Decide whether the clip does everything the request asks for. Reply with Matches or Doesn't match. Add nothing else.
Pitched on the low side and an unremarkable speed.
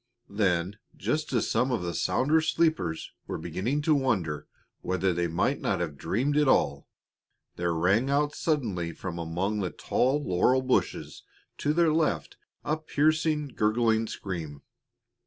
Matches